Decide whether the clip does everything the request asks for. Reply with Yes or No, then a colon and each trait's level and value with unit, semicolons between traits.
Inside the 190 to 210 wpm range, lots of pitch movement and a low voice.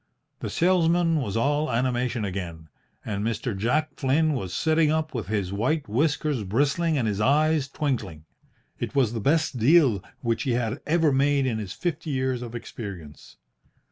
No: average, 165 wpm; wide, 5.8 semitones; low, 130 Hz